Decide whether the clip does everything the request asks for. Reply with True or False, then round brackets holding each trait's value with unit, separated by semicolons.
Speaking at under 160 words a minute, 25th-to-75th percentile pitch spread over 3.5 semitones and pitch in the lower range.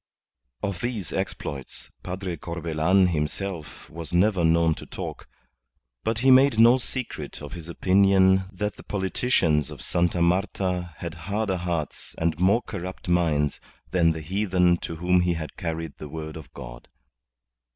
False (150 wpm; 3.1 semitones; 90 Hz)